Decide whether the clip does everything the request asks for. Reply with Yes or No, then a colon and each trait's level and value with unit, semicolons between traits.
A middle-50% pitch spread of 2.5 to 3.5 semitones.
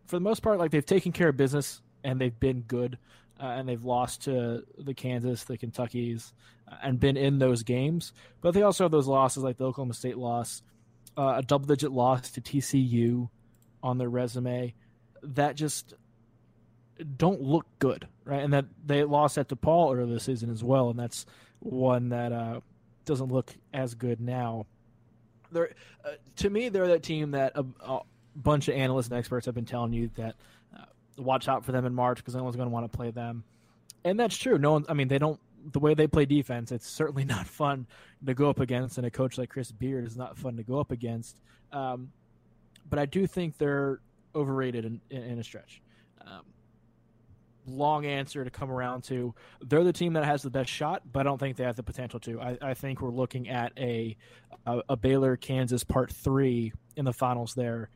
Yes: average, 2.8 semitones